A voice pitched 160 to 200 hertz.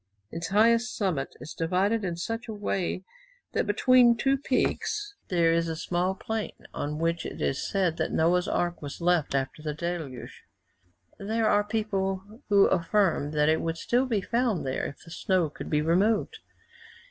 Yes: medium, 185 Hz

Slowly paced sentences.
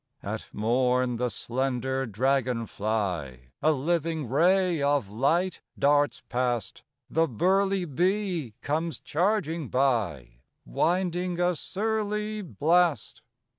Yes: slow, 100 wpm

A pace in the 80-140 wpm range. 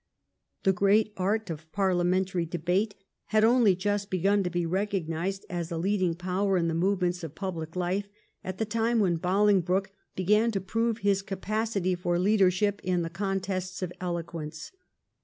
No: average, 160 wpm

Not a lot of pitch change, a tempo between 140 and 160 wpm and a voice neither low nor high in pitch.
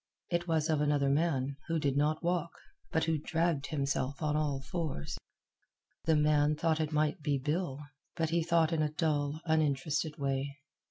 No: narrow, 2.3 semitones; average, 170 wpm; medium, 150 Hz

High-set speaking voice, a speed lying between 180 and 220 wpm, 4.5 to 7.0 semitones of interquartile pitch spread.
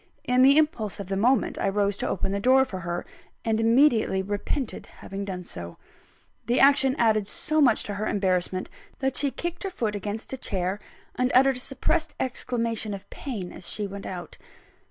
Yes: high, 220 Hz; average, 190 wpm; average, 5.1 semitones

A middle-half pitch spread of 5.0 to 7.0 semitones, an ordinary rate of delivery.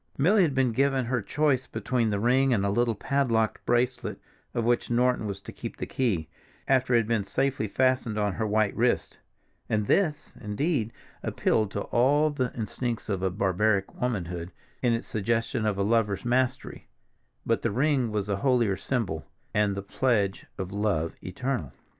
No: average, 4.1 semitones; average, 170 wpm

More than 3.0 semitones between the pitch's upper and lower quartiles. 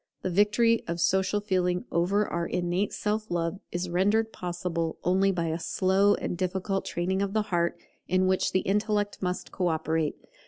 No: average, 2.7 semitones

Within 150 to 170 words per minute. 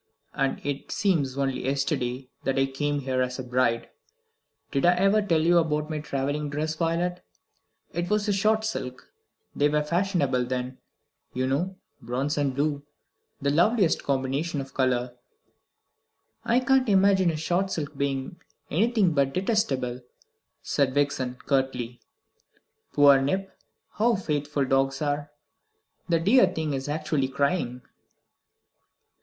No: slow, 135 wpm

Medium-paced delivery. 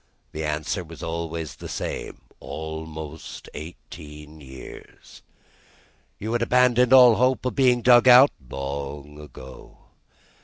No: slow, 115 wpm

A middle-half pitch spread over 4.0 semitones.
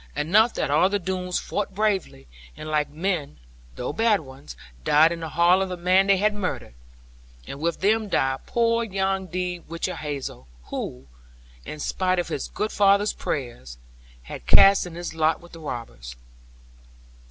Yes: average, 4.7 semitones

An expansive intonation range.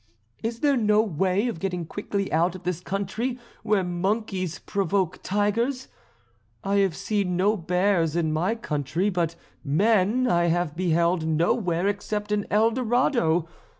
No: average, 3.7 semitones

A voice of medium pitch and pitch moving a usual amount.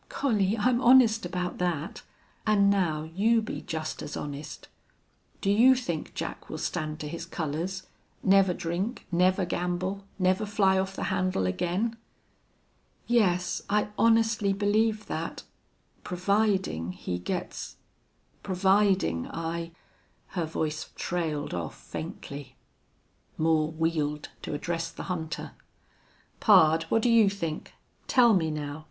Yes: medium, 180 Hz; average, 4.4 semitones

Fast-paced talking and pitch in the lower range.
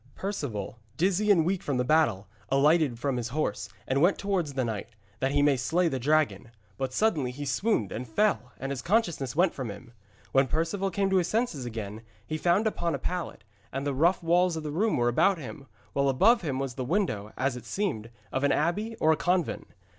No: fast, 215 wpm; medium, 145 Hz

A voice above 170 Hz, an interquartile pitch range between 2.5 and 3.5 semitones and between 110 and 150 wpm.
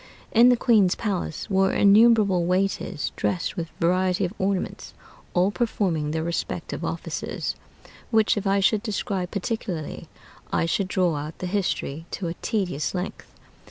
Yes: high, 190 Hz; average, 3.0 semitones; average, 145 wpm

